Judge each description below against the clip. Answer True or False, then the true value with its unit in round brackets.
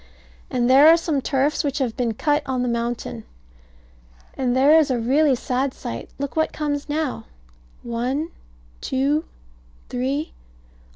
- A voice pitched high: True (270 Hz)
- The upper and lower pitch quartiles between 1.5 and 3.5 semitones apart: True (3.1 semitones)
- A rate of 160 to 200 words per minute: False (140 wpm)